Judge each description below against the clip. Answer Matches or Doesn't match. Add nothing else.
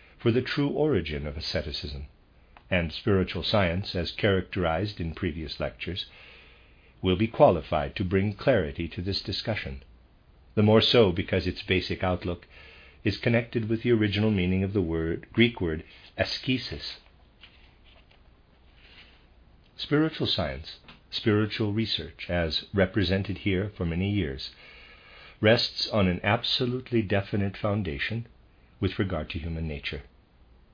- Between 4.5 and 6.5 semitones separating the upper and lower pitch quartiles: Matches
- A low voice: Matches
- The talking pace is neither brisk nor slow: Doesn't match